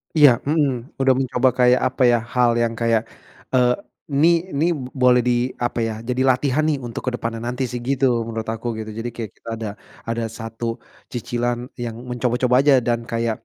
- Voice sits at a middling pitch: No, low, 125 Hz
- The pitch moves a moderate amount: No, narrow, 2.0 semitones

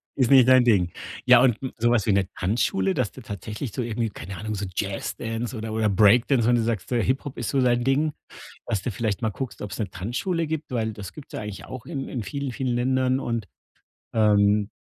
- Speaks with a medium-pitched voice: No, low, 115 Hz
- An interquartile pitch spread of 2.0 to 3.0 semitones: No, average, 3.6 semitones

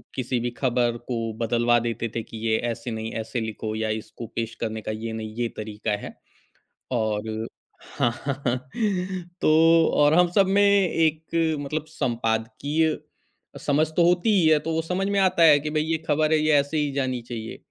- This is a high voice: No, low, 130 Hz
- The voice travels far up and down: Yes, wide, 5.9 semitones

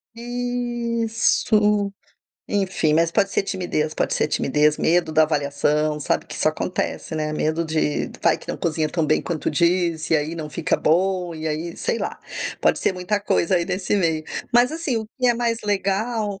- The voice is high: No, medium, 175 Hz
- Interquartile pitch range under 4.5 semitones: No, average, 5.1 semitones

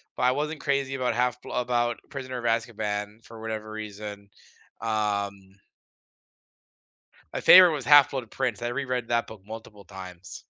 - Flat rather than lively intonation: No, average, 3.4 semitones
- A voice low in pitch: Yes, low, 115 Hz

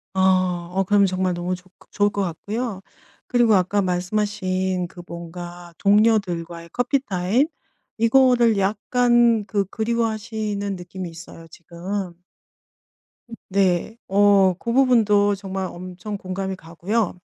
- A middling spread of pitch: Yes, average, 3.4 semitones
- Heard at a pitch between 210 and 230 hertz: No, high, 195 Hz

